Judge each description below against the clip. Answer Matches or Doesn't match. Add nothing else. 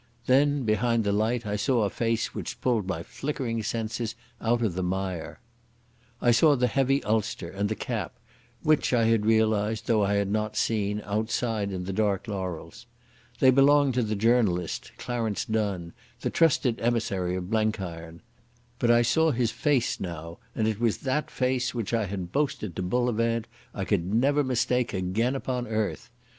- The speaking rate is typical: Matches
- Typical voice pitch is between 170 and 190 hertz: Doesn't match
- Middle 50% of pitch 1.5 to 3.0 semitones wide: Doesn't match